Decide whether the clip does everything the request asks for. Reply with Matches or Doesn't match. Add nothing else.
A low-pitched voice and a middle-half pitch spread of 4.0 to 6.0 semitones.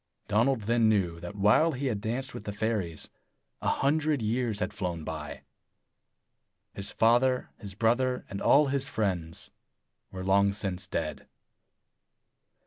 Matches